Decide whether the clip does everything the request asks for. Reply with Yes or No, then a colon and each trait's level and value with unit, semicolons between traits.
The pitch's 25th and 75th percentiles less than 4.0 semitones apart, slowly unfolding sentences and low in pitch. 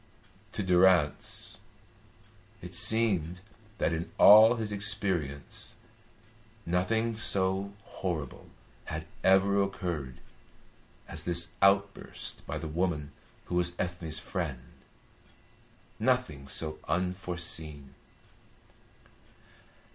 Yes: average, 3.6 semitones; slow, 85 wpm; very low, 90 Hz